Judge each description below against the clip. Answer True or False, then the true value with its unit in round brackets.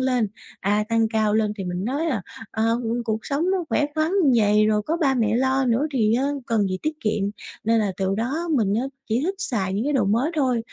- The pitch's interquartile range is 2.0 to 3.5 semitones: False (4.2 semitones)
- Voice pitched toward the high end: True (230 Hz)